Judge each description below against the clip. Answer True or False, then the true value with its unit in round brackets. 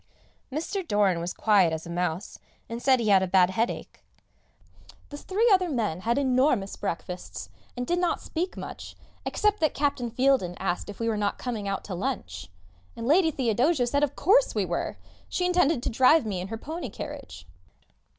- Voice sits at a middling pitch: False (235 Hz)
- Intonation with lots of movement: True (7.7 semitones)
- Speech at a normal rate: True (190 wpm)